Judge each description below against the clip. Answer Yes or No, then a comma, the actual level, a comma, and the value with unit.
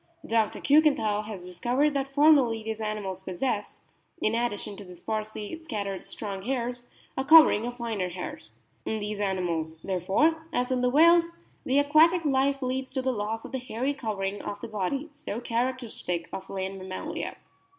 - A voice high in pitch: Yes, high, 230 Hz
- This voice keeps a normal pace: Yes, average, 165 wpm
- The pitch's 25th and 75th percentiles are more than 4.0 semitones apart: Yes, average, 5.2 semitones